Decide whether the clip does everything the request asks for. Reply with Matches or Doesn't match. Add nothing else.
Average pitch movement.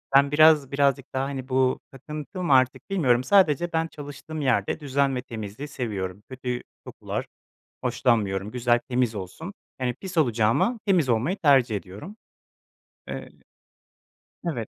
Matches